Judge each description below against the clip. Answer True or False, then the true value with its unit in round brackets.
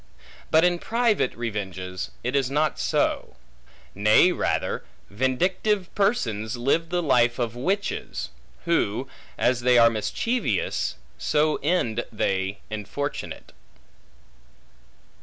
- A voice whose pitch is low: True (130 Hz)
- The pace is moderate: False (100 wpm)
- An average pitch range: False (7.9 semitones)